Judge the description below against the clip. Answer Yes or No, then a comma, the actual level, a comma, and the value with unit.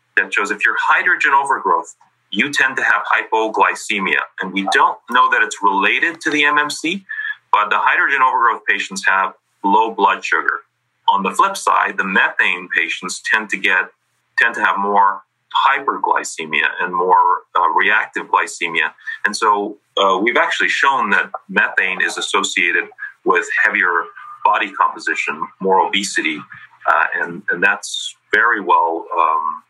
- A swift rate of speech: No, average, 145 wpm